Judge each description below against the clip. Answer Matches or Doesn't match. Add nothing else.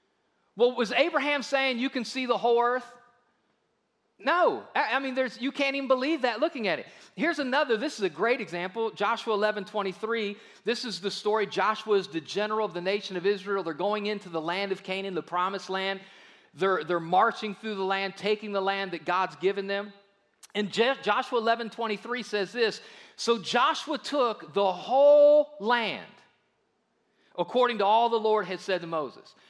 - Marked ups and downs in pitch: Doesn't match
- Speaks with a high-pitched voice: Matches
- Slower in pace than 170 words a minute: Doesn't match